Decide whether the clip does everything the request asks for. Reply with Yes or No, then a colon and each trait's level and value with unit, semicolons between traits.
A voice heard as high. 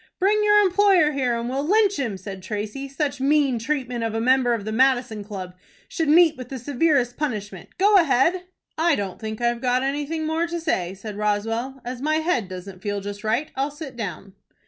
Yes: very high, 255 Hz